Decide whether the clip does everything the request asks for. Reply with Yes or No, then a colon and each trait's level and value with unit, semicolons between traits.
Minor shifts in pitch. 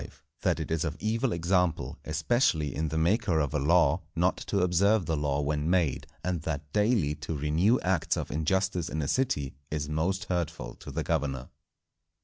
No: average, 3.7 semitones